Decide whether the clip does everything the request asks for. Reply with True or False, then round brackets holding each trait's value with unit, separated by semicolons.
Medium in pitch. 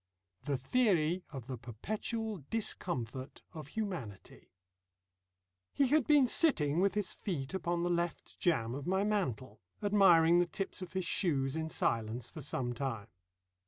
True (170 Hz)